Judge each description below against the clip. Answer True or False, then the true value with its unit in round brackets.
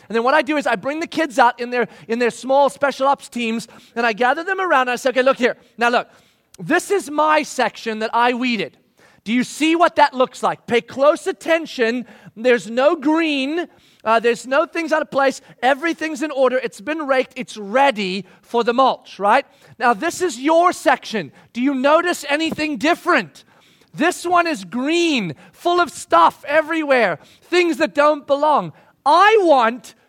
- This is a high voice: True (270 Hz)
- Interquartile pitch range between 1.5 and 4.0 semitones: False (4.8 semitones)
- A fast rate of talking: False (190 wpm)